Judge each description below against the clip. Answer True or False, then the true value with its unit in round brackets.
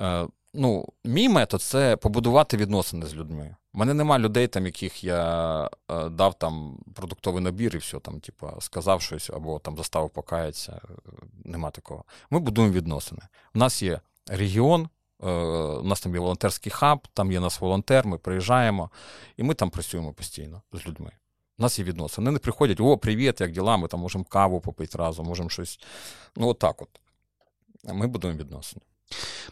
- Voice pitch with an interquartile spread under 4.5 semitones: False (5.3 semitones)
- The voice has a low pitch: True (95 Hz)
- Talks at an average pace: False (165 wpm)